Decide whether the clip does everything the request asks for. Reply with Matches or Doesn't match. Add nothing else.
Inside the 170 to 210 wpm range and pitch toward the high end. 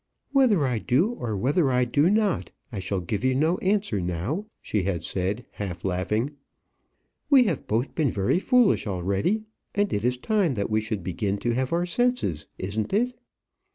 Doesn't match